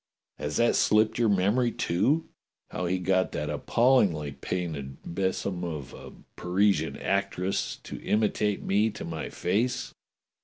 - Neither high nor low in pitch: No, very low, 95 Hz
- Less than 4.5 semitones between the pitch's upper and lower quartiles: Yes, average, 3.9 semitones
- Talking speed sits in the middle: No, slow, 130 wpm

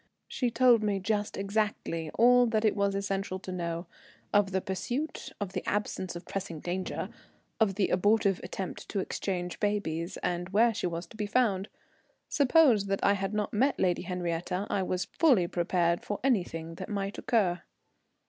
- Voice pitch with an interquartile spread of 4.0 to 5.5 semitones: No, average, 3.0 semitones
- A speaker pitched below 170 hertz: No, high, 195 Hz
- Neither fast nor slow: Yes, average, 170 wpm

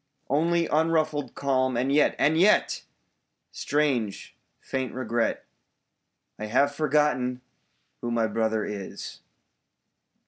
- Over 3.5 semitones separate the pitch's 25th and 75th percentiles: Yes, average, 4.2 semitones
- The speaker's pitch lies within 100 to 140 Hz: Yes, low, 135 Hz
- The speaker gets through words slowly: Yes, slow, 115 wpm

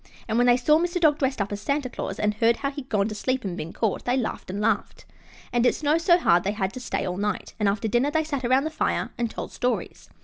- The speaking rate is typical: No, fast, 280 wpm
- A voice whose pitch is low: No, high, 245 Hz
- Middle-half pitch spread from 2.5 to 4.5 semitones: No, average, 5.3 semitones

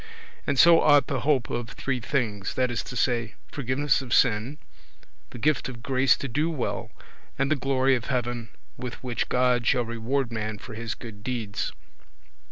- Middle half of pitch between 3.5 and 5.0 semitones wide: No, average, 2.8 semitones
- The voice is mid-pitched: No, low, 125 Hz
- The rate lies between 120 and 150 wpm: No, average, 175 wpm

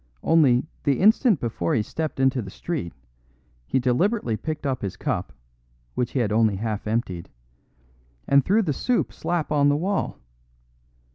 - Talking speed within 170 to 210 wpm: No, average, 155 wpm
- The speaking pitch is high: No, low, 135 Hz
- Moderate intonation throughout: No, wide, 6.3 semitones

